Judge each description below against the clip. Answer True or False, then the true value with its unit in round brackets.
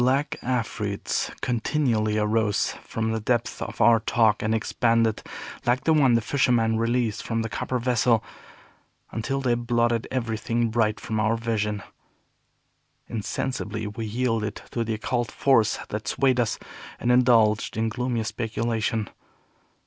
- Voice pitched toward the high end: False (115 Hz)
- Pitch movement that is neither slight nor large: False (1.9 semitones)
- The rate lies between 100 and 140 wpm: True (135 wpm)